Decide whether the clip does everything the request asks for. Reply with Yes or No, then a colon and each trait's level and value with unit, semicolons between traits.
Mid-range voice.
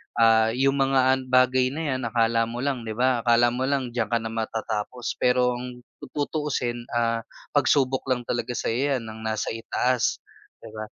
No: low, 125 Hz